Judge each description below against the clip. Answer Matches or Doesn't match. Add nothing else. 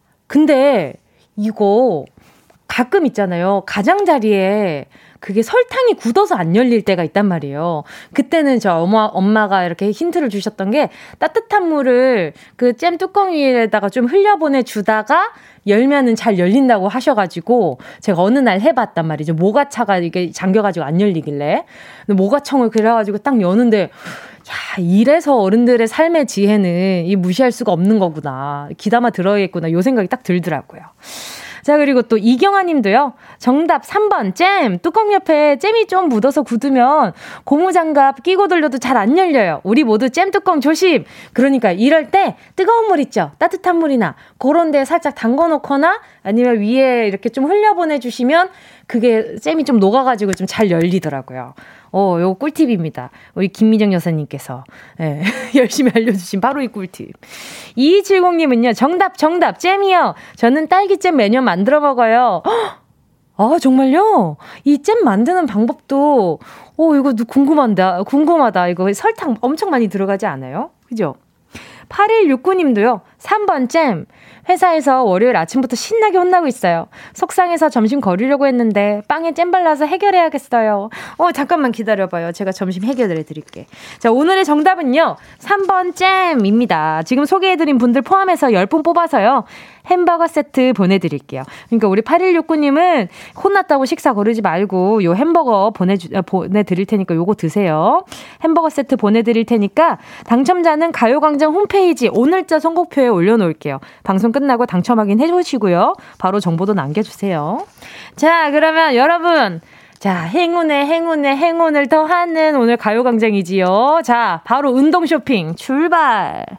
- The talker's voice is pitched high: Matches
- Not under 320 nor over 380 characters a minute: Matches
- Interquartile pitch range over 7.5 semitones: Matches